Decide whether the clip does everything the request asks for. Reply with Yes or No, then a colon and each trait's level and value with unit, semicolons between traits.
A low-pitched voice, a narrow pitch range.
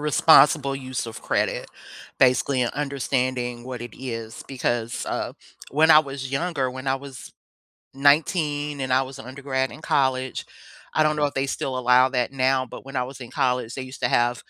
Yes: low, 130 Hz; narrow, 1.7 semitones